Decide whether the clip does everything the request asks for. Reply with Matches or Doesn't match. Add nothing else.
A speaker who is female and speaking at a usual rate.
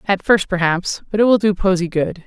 Doesn't match